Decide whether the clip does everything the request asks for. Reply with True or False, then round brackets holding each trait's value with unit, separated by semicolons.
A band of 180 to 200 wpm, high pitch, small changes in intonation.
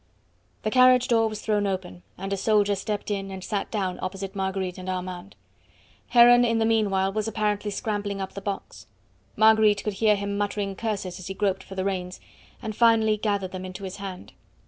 True (190 wpm; 200 Hz; 2.1 semitones)